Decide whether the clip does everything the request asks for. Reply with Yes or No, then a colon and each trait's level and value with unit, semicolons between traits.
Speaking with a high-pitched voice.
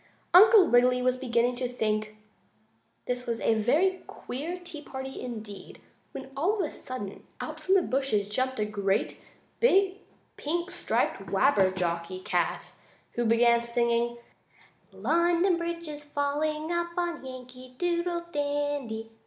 Yes: very high, 260 Hz